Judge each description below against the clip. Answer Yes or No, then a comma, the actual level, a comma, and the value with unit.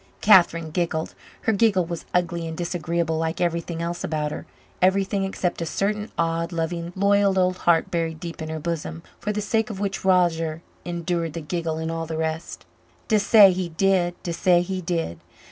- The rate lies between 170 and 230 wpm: Yes, average, 180 wpm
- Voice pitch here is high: No, medium, 170 Hz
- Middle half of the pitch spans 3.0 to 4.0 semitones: No, narrow, 2.5 semitones